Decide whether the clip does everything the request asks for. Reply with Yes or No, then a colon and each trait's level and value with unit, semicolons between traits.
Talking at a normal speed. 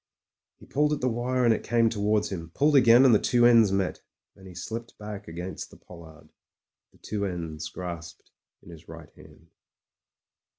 Yes: average, 185 wpm